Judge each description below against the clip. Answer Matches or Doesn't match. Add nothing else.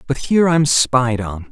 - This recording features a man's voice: Matches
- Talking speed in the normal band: Matches